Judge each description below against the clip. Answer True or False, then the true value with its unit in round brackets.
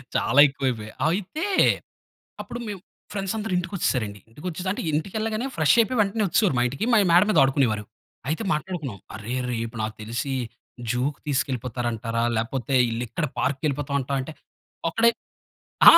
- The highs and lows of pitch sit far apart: True (7.8 semitones)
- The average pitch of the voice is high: False (140 Hz)